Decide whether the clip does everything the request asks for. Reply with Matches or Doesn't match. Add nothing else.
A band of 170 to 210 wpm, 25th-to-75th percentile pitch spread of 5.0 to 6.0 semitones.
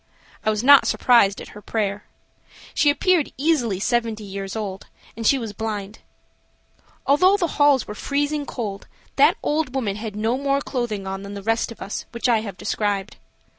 Matches